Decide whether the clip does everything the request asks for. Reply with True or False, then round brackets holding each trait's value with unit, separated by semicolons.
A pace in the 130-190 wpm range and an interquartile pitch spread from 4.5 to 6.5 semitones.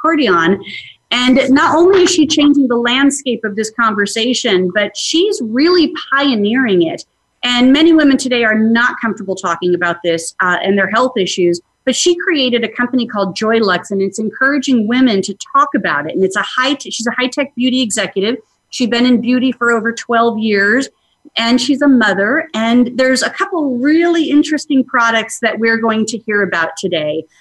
True (180 wpm; 4.8 semitones)